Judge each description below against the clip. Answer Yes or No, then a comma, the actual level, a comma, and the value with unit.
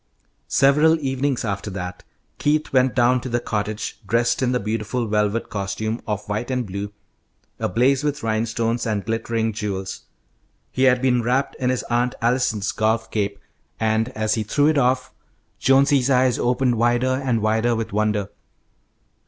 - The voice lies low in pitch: Yes, low, 115 Hz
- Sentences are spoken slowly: No, average, 155 wpm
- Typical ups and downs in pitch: Yes, average, 3.1 semitones